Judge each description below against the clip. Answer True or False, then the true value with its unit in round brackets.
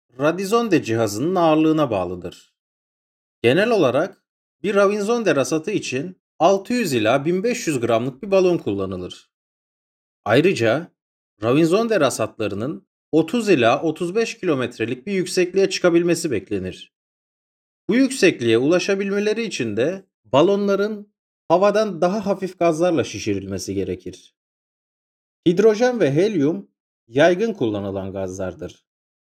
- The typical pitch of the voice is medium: True (170 Hz)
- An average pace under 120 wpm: True (95 wpm)